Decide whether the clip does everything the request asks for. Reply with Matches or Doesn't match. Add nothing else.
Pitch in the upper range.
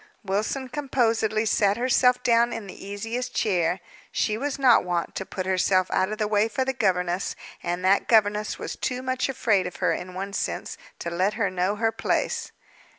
Matches